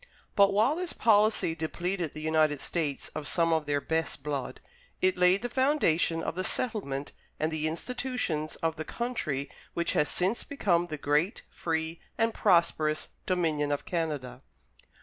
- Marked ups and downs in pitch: No, average, 4.3 semitones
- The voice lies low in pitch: No, medium, 165 Hz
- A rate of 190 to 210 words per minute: No, average, 155 wpm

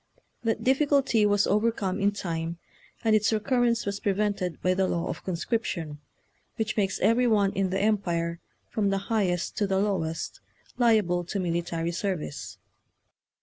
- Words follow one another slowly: No, average, 150 wpm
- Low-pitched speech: No, high, 200 Hz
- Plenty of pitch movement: No, average, 3.6 semitones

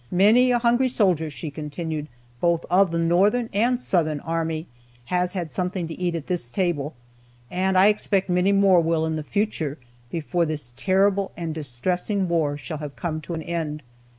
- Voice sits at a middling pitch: Yes, medium, 170 Hz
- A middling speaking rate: Yes, average, 180 wpm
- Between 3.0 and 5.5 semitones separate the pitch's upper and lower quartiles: Yes, average, 3.5 semitones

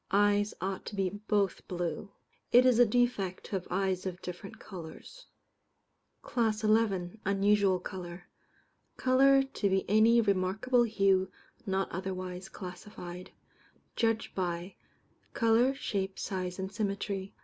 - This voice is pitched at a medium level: No, high, 195 Hz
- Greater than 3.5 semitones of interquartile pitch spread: No, average, 2.9 semitones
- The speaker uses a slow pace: Yes, slow, 125 wpm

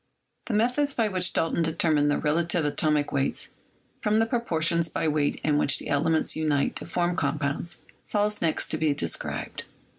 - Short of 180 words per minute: Yes, average, 170 wpm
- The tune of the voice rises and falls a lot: No, average, 3.9 semitones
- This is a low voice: No, medium, 160 Hz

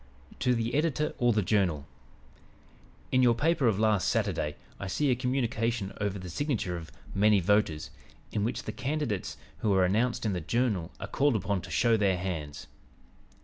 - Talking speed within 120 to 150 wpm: No, average, 175 wpm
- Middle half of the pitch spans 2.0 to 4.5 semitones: No, average, 4.9 semitones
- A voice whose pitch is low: Yes, low, 105 Hz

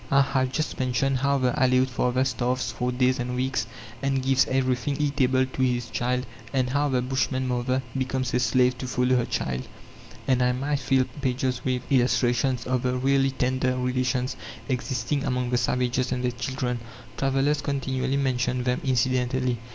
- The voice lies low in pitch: Yes, low, 130 Hz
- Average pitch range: No, narrow, 1.1 semitones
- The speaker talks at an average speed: Yes, average, 170 wpm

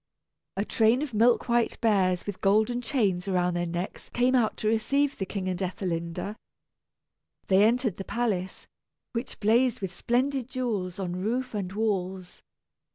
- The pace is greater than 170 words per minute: No, average, 155 wpm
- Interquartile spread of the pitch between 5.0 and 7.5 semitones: No, average, 4.5 semitones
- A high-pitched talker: Yes, high, 210 Hz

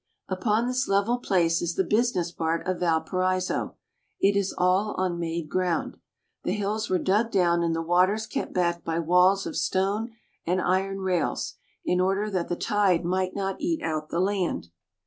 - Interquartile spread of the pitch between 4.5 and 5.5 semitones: No, average, 2.7 semitones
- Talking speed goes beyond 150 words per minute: Yes, average, 175 wpm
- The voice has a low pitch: No, medium, 185 Hz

